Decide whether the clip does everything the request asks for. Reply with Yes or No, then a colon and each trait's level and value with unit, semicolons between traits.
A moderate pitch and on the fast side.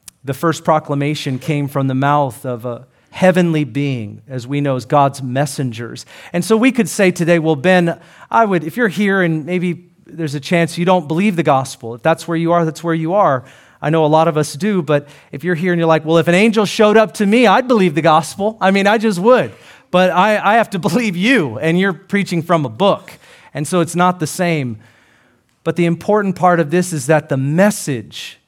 Yes: medium, 170 Hz; fast, 230 wpm